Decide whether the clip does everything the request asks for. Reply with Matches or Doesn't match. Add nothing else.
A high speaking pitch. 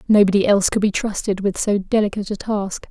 Matches